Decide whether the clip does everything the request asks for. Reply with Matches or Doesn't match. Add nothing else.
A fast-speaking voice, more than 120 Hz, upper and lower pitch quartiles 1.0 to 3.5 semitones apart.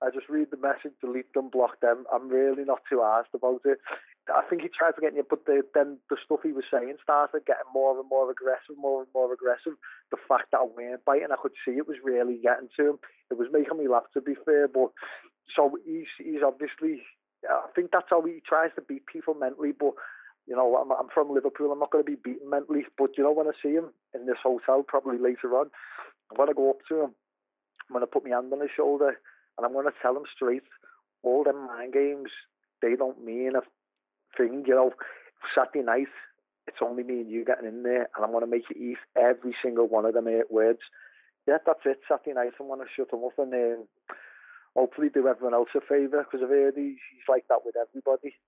Matches